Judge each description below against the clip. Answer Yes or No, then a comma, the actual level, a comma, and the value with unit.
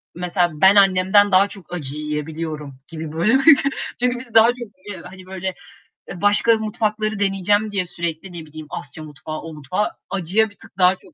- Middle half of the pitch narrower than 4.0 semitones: No, average, 4.4 semitones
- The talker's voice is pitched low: No, medium, 185 Hz